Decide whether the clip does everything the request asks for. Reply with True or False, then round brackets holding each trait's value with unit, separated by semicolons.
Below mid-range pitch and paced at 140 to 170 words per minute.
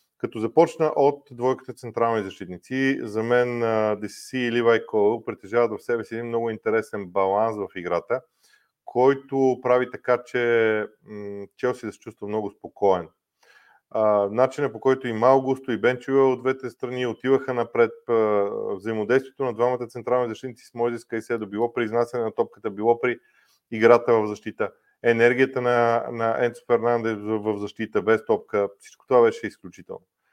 True (120 Hz; 150 wpm)